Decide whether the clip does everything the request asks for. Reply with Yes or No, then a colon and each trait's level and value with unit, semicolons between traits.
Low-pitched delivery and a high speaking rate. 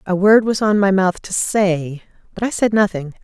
No: high, 195 Hz; fast, 220 wpm